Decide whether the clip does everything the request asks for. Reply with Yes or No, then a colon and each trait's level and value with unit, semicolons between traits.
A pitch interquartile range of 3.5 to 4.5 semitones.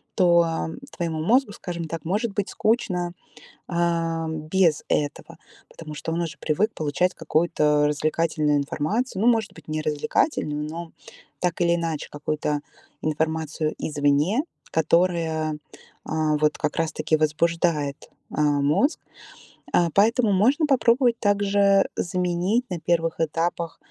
Yes: average, 3.8 semitones